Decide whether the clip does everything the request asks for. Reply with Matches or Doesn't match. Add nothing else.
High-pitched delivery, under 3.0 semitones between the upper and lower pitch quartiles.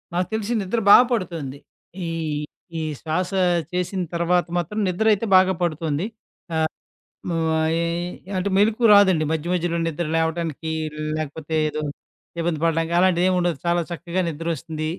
Doesn't match